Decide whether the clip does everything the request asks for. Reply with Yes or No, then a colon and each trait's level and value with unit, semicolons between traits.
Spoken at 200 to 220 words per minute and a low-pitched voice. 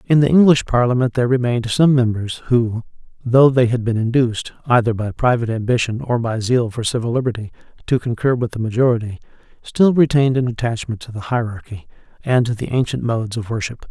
No: average, 185 wpm; low, 120 Hz